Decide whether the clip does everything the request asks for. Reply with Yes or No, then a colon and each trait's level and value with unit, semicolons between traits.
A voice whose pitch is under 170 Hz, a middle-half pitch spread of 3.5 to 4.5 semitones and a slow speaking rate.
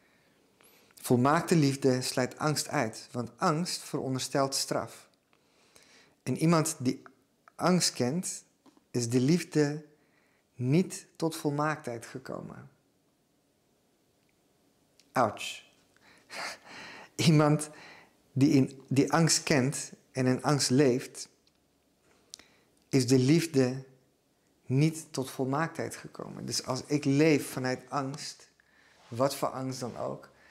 No: medium, 140 Hz; average, 3.0 semitones; slow, 100 wpm